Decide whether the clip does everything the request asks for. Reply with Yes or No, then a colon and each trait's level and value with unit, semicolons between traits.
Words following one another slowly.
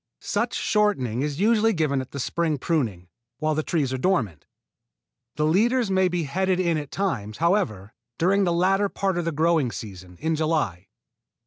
No: average, 175 wpm